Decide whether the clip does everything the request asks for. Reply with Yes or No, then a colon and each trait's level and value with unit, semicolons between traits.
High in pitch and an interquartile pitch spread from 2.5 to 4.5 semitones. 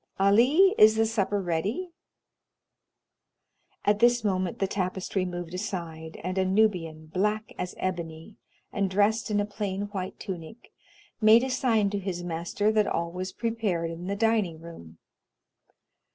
Yes: high, 195 Hz; average, 3.6 semitones